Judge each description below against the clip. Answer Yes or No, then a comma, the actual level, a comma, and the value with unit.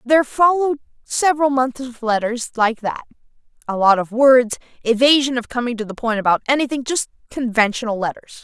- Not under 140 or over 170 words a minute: Yes, average, 165 wpm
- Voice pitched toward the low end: No, high, 245 Hz